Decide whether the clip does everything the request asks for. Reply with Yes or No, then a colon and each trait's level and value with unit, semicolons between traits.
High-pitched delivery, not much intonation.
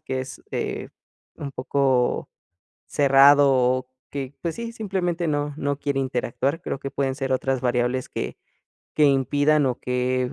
No: low, 135 Hz; narrow, 2.1 semitones